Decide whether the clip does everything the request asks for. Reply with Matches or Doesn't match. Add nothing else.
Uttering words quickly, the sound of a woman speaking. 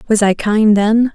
Matches